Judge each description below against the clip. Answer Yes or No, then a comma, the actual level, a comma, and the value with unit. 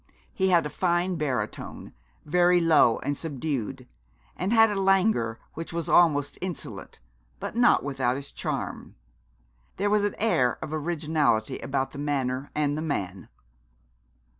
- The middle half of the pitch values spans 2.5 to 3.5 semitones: No, average, 4.7 semitones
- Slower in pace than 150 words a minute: Yes, average, 140 wpm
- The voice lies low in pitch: No, medium, 155 Hz